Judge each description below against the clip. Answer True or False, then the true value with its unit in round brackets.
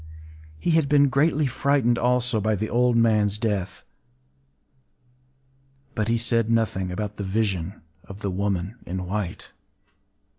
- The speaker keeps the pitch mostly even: False (3.8 semitones)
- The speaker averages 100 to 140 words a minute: True (135 wpm)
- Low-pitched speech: True (110 Hz)